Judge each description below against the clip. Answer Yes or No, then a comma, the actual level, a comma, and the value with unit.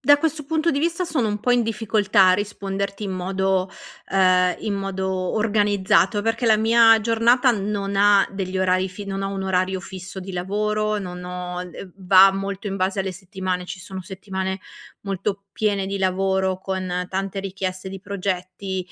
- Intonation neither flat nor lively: No, narrow, 1.9 semitones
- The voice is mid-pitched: No, high, 195 Hz